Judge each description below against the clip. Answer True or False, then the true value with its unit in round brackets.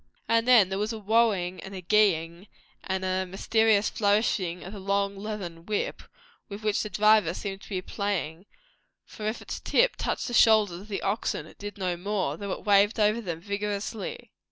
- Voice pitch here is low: False (200 Hz)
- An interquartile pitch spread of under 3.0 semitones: True (2.4 semitones)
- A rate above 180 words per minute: True (200 wpm)